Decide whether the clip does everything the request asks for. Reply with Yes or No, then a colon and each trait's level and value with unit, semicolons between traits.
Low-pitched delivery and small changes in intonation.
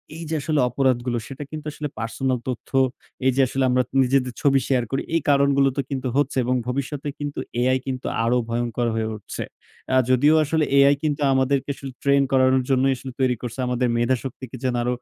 Yes: low, 130 Hz; narrow, 1.8 semitones